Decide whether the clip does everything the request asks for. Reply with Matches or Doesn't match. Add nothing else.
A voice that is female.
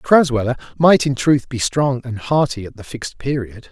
Doesn't match